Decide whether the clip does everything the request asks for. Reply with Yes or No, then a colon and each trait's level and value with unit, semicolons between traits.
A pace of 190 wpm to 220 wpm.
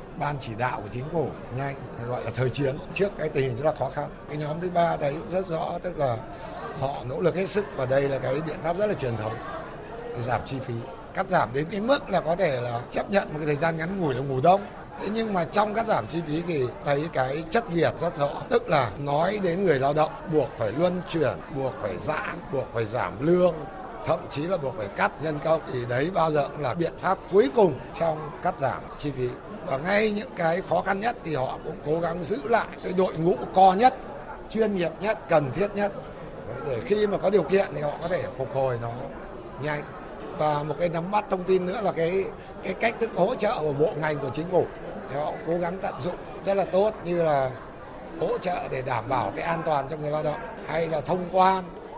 No: average, 240 wpm